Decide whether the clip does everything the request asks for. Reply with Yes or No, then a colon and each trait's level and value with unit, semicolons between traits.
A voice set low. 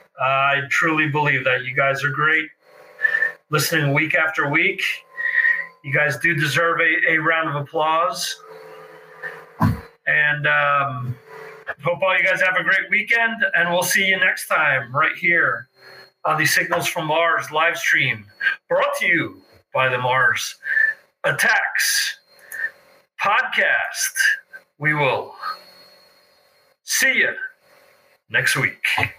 No: medium, 175 Hz